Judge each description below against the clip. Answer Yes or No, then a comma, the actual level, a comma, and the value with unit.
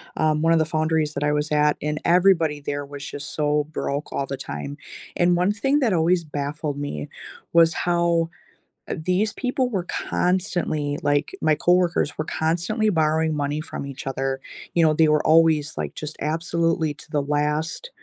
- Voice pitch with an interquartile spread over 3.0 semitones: No, average, 2.7 semitones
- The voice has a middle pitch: Yes, medium, 155 Hz